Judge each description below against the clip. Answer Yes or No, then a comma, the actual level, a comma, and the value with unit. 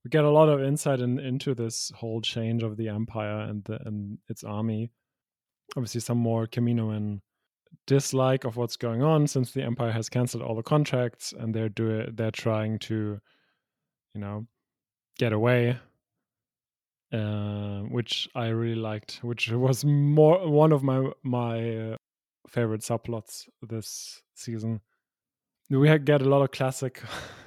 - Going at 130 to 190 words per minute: Yes, average, 155 wpm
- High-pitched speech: No, low, 120 Hz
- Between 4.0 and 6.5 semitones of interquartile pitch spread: No, average, 2.9 semitones